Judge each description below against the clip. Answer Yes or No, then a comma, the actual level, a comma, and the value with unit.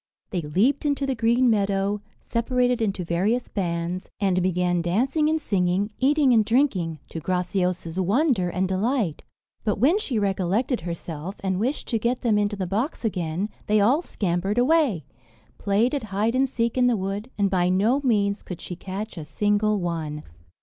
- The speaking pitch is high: Yes, high, 205 Hz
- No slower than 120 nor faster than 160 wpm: No, average, 170 wpm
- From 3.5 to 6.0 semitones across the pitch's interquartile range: Yes, average, 5.0 semitones